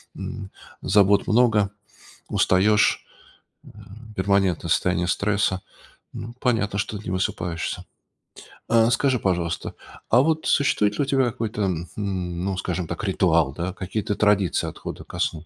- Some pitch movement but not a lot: Yes, average, 3.0 semitones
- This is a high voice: No, low, 100 Hz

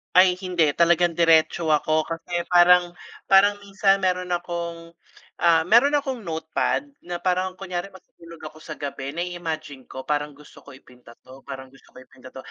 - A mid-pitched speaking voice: Yes, medium, 170 Hz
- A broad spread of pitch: No, average, 3.0 semitones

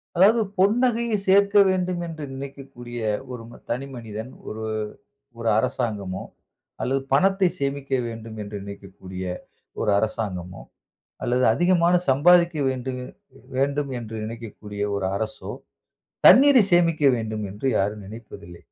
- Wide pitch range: Yes, wide, 8.1 semitones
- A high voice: No, low, 130 Hz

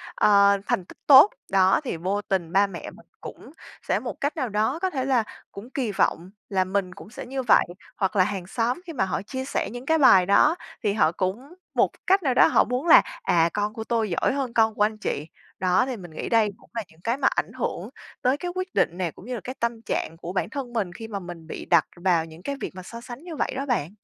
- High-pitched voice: Yes, high, 215 Hz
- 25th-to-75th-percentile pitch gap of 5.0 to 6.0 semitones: Yes, wide, 5.6 semitones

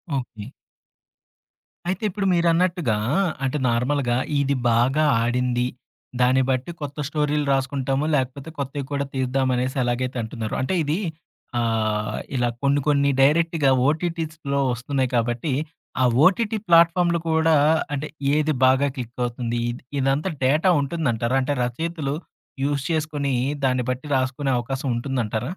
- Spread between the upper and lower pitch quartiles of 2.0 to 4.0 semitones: Yes, average, 3.5 semitones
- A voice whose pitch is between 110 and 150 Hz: Yes, low, 135 Hz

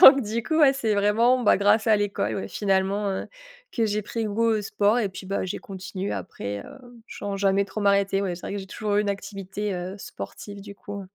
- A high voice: Yes, high, 205 Hz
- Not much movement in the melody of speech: Yes, narrow, 1.9 semitones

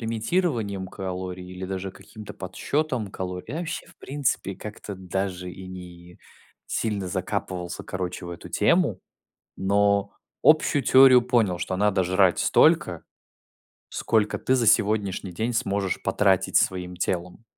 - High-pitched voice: No, very low, 95 Hz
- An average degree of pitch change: Yes, average, 3.3 semitones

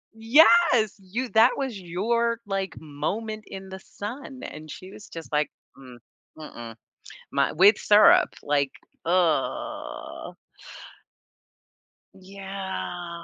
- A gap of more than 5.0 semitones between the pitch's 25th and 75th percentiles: Yes, wide, 5.5 semitones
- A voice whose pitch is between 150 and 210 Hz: Yes, high, 190 Hz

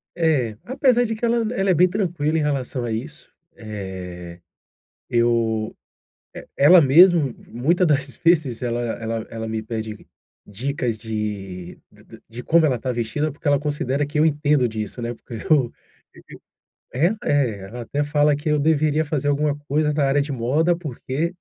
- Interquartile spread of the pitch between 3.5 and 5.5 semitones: Yes, average, 5.0 semitones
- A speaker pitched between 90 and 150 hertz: Yes, medium, 140 Hz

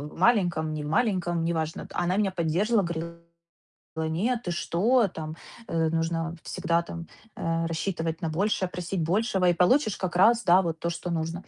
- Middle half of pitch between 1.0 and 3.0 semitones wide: Yes, narrow, 2.5 semitones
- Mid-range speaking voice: Yes, medium, 170 Hz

